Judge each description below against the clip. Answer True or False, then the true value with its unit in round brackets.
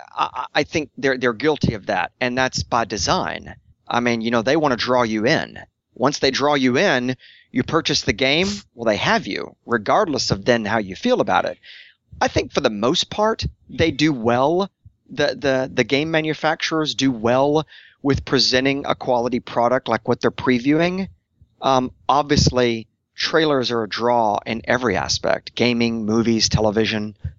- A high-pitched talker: False (130 Hz)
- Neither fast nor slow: True (175 wpm)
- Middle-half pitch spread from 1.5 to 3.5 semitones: False (4.0 semitones)